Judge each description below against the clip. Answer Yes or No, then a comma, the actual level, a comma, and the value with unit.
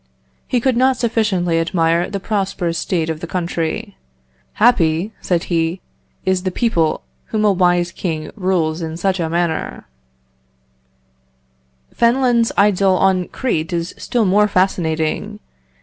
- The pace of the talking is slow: Yes, slow, 130 wpm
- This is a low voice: No, medium, 185 Hz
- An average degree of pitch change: Yes, average, 3.9 semitones